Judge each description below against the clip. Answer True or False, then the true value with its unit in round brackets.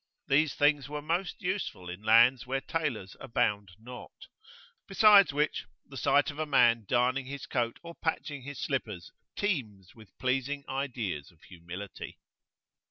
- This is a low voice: True (130 Hz)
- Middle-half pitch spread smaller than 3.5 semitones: False (5.1 semitones)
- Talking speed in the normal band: True (145 wpm)